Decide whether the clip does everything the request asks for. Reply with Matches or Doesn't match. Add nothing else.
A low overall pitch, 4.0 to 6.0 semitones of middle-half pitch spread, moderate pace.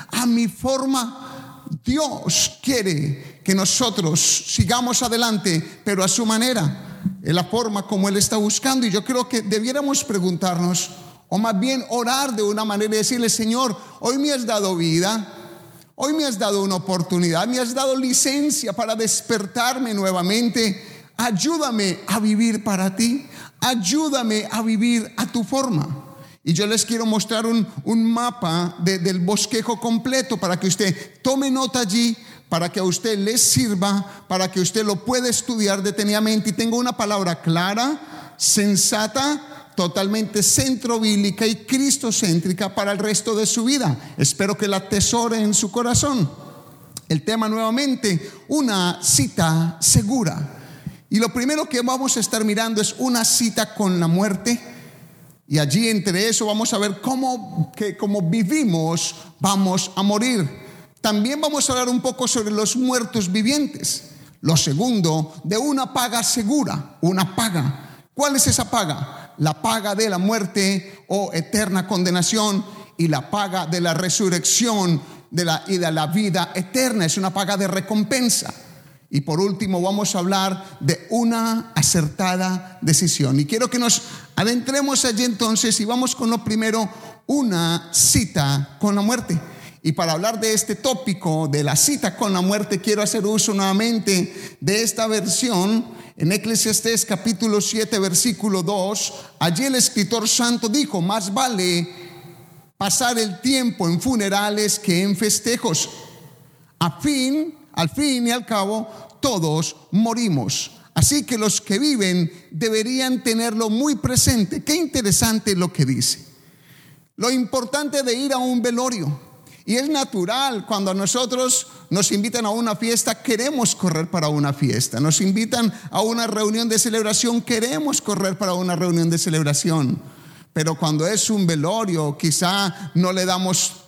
Doesn't match